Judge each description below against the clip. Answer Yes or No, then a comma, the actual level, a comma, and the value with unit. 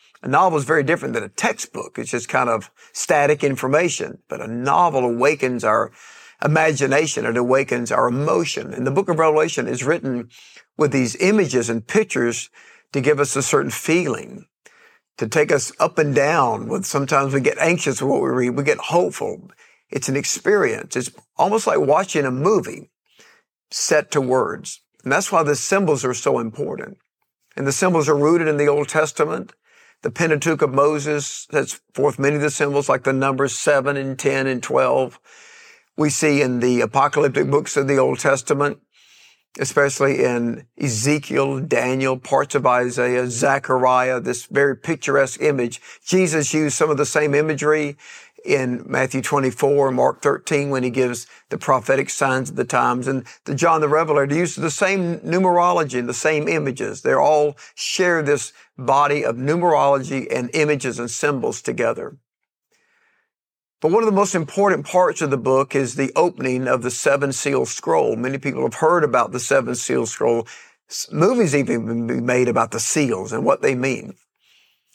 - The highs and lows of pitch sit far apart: No, average, 3.9 semitones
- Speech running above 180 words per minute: No, average, 170 wpm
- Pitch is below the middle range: No, medium, 145 Hz